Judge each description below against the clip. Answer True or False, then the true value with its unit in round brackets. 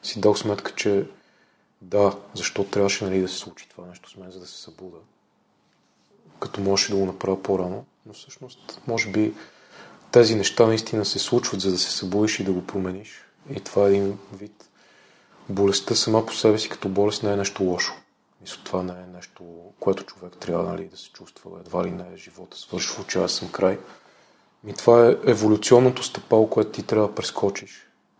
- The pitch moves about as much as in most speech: False (2.3 semitones)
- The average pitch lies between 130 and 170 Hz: False (100 Hz)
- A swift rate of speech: True (195 wpm)